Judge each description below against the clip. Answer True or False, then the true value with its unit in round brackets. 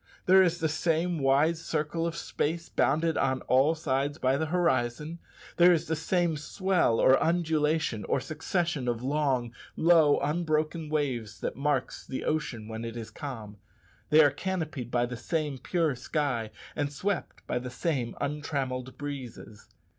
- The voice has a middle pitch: True (150 Hz)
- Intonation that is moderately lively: True (4.1 semitones)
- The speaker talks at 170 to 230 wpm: False (155 wpm)